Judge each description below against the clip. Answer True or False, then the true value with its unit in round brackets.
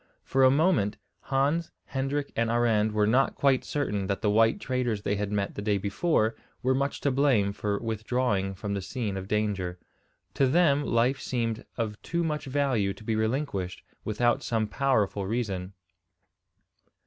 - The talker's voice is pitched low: True (115 Hz)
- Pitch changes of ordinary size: True (4.7 semitones)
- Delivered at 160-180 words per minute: True (165 wpm)